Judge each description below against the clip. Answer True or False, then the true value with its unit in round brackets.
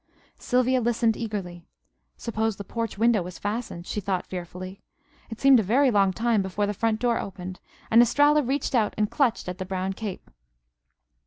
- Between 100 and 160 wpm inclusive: False (175 wpm)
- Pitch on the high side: True (215 Hz)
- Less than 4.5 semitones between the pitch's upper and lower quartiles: True (3.9 semitones)